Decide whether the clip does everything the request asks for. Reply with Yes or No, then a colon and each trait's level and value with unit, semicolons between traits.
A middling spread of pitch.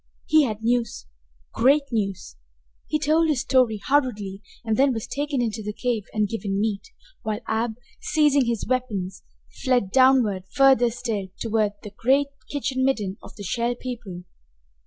Yes: average, 4.0 semitones